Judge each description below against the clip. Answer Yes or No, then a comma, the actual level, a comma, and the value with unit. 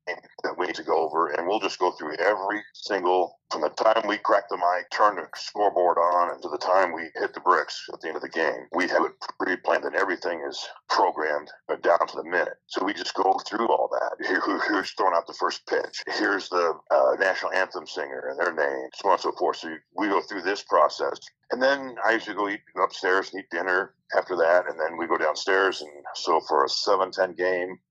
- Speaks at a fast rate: Yes, fast, 235 wpm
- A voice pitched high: Yes, very high, 375 Hz